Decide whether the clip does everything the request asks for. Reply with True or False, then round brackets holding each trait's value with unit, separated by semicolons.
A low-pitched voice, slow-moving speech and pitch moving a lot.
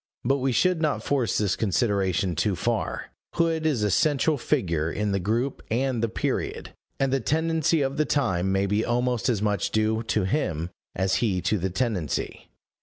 False (110 Hz; 180 wpm; 5.9 semitones)